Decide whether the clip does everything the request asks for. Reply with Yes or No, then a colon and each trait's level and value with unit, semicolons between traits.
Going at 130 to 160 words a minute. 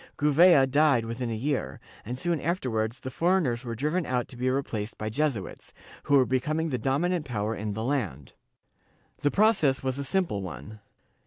No: average, 175 wpm